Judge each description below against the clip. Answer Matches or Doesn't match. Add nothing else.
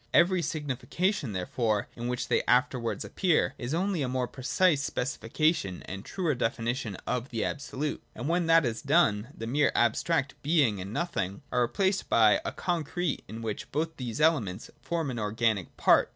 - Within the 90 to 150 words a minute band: Doesn't match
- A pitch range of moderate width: Doesn't match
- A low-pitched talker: Matches